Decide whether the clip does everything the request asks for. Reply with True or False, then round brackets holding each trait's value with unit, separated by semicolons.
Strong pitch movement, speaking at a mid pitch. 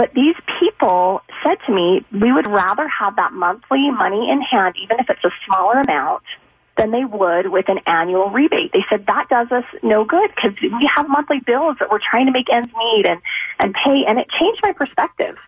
False (6.9 semitones; 245 Hz)